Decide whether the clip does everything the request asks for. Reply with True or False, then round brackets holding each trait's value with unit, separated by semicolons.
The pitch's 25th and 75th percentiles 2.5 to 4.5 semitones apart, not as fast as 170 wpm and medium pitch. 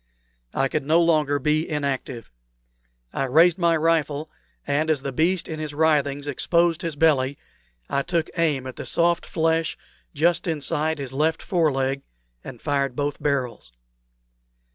True (2.8 semitones; 150 wpm; 150 Hz)